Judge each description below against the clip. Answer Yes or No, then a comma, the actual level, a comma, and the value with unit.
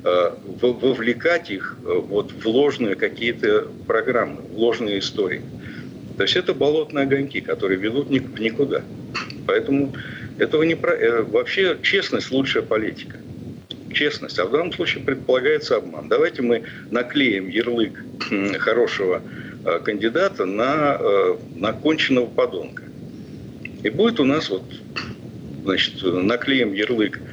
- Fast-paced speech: No, average, 115 wpm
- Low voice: No, very high, 395 Hz